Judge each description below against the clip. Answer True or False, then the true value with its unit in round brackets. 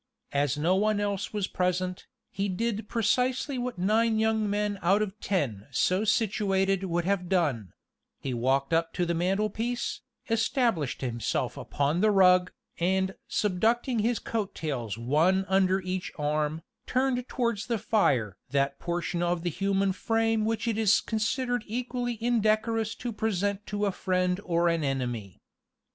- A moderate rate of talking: True (150 wpm)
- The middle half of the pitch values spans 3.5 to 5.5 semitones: True (4.4 semitones)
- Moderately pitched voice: False (195 Hz)